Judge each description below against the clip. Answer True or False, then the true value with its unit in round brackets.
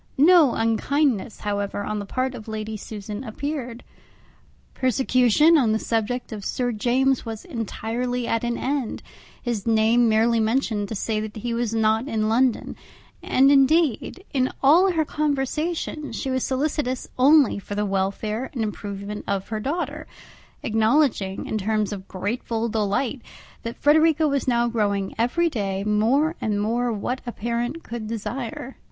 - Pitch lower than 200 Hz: False (235 Hz)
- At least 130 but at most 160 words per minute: True (150 wpm)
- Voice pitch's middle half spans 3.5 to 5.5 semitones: True (3.8 semitones)